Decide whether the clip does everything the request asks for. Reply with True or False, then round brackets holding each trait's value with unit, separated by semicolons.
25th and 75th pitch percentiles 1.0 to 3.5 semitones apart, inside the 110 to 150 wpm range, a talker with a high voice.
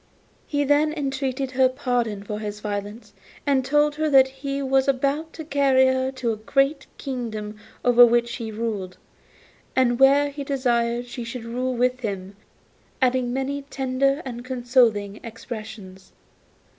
True (3.0 semitones; 145 wpm; 255 Hz)